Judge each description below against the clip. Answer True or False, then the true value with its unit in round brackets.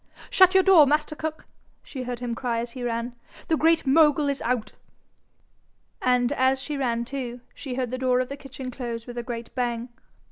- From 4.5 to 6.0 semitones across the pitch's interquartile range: False (2.8 semitones)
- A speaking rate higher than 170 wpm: True (200 wpm)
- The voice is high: True (255 Hz)